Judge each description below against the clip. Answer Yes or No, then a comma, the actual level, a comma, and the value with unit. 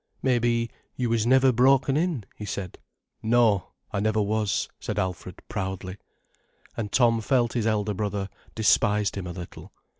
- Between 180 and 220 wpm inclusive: No, average, 150 wpm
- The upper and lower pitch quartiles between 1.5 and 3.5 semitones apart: Yes, average, 3.2 semitones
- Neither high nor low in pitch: No, low, 110 Hz